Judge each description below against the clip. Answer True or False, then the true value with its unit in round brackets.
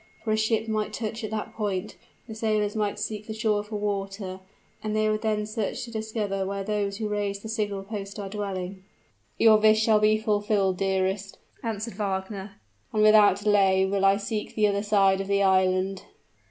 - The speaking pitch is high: True (210 Hz)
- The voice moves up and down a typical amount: False (1.6 semitones)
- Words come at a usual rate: True (190 wpm)